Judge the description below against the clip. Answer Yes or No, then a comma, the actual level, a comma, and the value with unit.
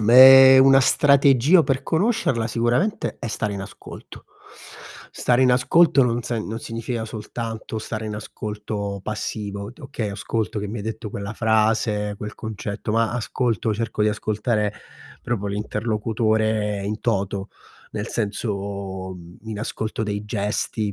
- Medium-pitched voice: No, low, 110 Hz